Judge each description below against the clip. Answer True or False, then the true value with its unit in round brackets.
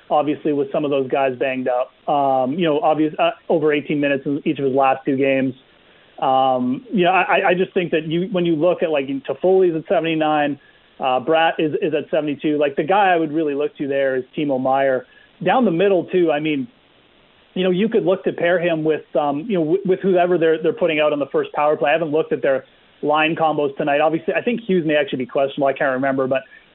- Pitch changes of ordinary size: True (3.7 semitones)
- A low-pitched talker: False (150 Hz)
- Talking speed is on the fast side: True (245 wpm)